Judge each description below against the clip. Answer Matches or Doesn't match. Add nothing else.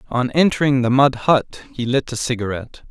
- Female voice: Doesn't match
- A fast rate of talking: Doesn't match